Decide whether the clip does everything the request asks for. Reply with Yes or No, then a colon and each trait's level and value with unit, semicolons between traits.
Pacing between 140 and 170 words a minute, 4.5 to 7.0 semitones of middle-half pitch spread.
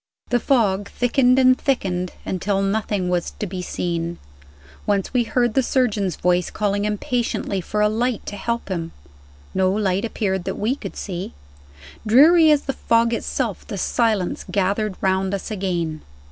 No: average, 160 wpm; average, 4.1 semitones